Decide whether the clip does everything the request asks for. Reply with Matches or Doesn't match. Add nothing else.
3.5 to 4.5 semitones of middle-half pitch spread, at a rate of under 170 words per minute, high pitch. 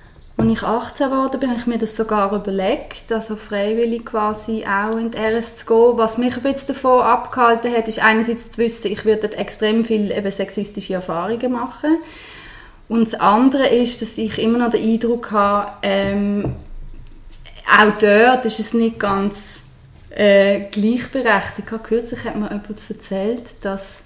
Doesn't match